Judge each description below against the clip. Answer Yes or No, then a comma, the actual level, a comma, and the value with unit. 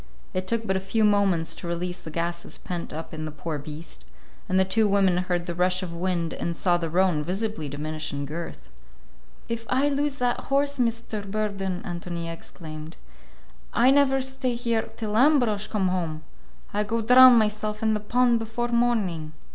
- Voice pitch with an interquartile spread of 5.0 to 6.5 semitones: Yes, average, 5.3 semitones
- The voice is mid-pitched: No, high, 195 Hz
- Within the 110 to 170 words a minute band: No, average, 180 wpm